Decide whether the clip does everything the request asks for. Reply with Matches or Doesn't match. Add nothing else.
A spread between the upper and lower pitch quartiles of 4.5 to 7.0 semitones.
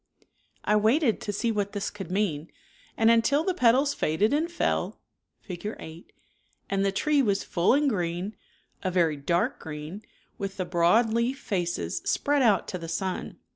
Matches